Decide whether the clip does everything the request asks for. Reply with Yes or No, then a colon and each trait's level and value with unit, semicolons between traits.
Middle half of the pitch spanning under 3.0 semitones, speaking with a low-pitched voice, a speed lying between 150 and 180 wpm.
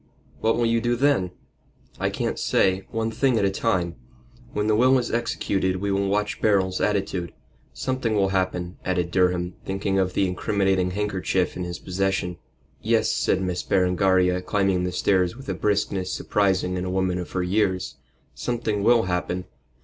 Yes: narrow, 2.4 semitones; very low, 95 Hz; average, 170 wpm